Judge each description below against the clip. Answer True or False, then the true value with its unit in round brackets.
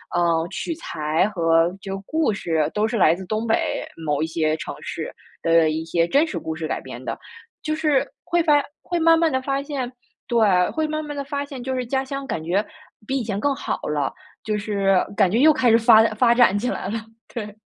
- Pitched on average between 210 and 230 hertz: True (220 Hz)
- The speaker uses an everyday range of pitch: False (8.3 semitones)